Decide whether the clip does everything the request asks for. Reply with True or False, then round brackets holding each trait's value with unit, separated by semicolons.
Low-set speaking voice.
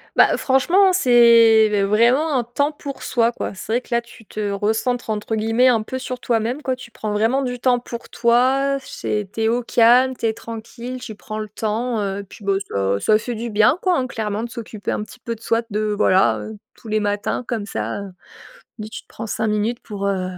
False (230 Hz)